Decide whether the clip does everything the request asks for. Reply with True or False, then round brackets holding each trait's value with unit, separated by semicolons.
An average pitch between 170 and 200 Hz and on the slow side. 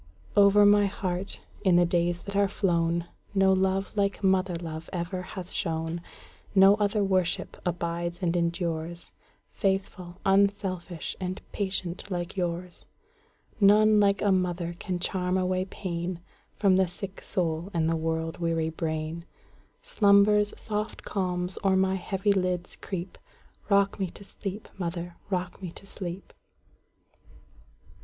True (185 Hz; 120 wpm)